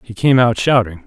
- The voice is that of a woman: No, male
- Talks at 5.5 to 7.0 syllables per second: No, 5.2 syllables/s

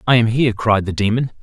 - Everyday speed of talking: No, fast, 250 wpm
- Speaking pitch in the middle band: No, low, 115 Hz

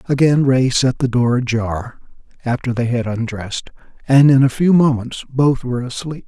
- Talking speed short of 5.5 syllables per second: Yes, 5.0 syllables/s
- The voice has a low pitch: Yes, low, 125 Hz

